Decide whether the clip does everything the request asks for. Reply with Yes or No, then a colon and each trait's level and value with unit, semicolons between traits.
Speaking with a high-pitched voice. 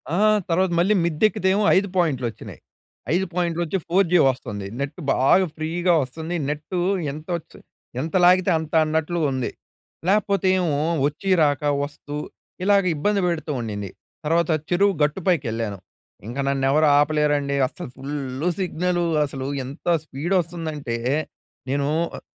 No: medium, 155 Hz